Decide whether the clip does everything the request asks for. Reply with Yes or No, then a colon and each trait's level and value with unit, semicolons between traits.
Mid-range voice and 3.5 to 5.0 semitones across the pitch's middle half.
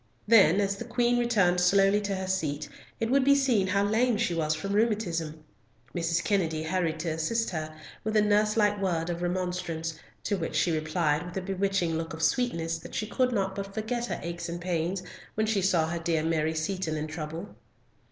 Yes: medium, 180 Hz; average, 4.2 semitones